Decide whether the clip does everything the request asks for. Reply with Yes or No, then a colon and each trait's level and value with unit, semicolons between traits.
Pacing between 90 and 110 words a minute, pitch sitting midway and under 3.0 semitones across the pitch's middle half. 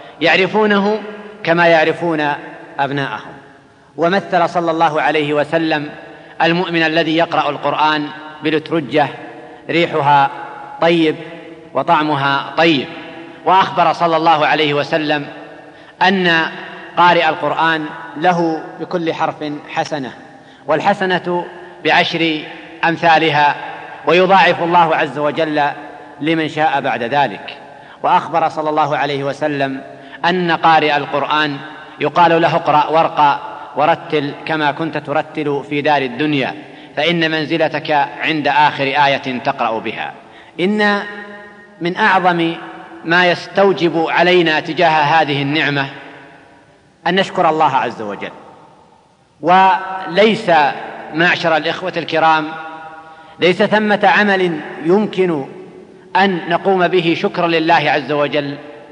Yes: average, 100 wpm; medium, 160 Hz; narrow, 2.5 semitones